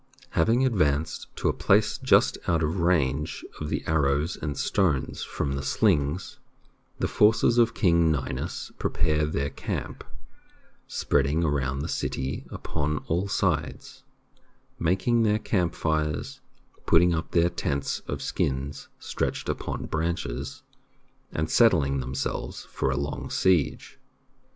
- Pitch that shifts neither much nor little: Yes, average, 3.7 semitones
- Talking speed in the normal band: No, slow, 125 wpm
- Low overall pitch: Yes, very low, 80 Hz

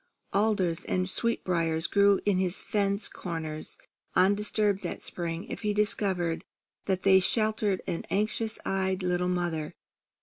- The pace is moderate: No, slow, 130 wpm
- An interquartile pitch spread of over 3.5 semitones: No, average, 2.7 semitones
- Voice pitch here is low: No, high, 190 Hz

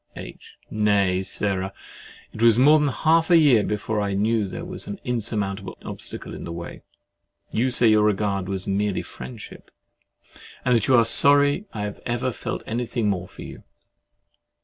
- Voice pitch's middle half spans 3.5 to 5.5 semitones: Yes, average, 4.2 semitones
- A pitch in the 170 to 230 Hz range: No, low, 110 Hz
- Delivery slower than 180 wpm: Yes, average, 170 wpm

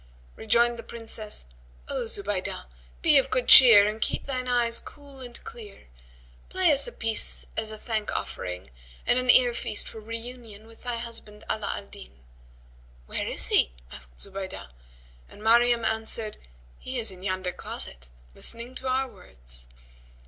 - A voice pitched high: Yes, high, 225 Hz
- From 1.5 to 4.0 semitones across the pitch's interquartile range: Yes, average, 3.3 semitones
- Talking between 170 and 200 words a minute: No, average, 155 wpm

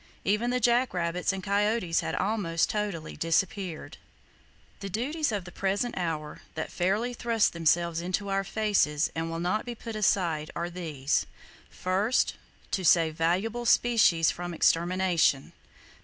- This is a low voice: No, medium, 185 Hz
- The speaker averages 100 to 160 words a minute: Yes, average, 140 wpm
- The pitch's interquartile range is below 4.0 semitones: No, average, 4.3 semitones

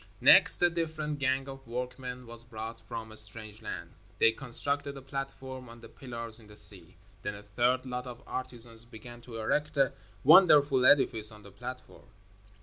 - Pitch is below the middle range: Yes, low, 125 Hz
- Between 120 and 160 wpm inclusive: No, average, 175 wpm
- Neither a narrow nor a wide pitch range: Yes, average, 3.3 semitones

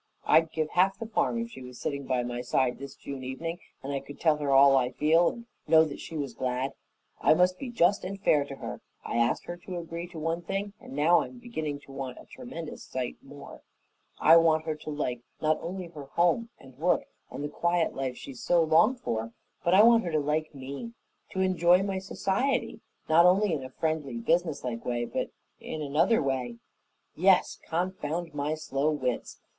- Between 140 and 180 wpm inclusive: No, fast, 205 wpm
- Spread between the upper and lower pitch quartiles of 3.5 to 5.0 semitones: Yes, average, 4.5 semitones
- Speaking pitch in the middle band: Yes, medium, 155 Hz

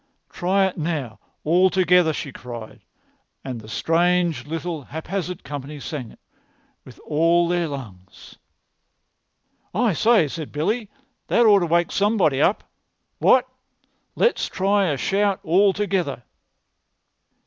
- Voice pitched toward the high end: No, medium, 170 Hz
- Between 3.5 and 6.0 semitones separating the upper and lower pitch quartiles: Yes, average, 4.9 semitones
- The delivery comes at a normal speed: No, slow, 125 wpm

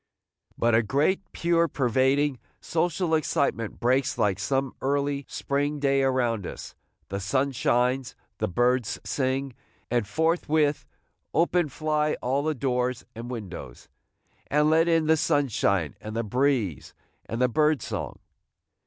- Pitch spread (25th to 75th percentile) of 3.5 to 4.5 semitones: Yes, average, 3.9 semitones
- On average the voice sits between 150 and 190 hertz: No, low, 135 Hz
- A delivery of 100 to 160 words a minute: Yes, slow, 135 wpm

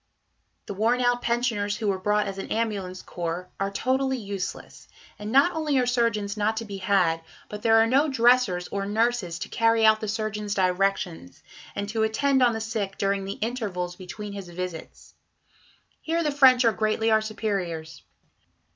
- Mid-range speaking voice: No, high, 215 Hz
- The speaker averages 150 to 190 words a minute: Yes, average, 175 wpm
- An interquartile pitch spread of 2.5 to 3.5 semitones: Yes, average, 3.1 semitones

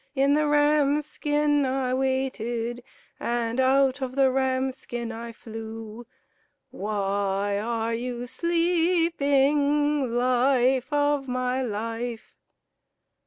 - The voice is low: No, very high, 260 Hz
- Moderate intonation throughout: Yes, average, 3.5 semitones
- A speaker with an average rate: No, slow, 100 wpm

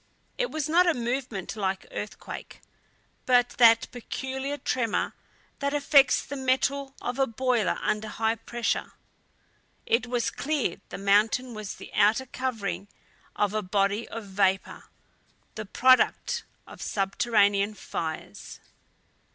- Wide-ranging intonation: No, average, 4.4 semitones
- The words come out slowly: Yes, slow, 125 wpm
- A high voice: Yes, high, 230 Hz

